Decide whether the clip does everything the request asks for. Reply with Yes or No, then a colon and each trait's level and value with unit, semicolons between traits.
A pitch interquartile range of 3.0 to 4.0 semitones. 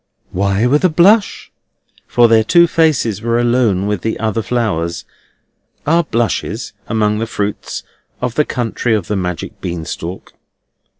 Yes: average, 3.6 semitones